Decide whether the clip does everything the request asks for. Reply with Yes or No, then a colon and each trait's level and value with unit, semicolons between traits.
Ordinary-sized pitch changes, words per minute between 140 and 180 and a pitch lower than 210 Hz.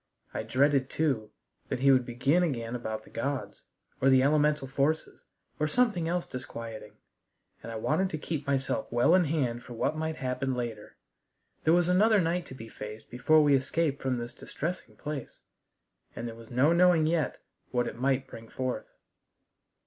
Yes: average, 4.6 semitones; average, 175 wpm; low, 135 Hz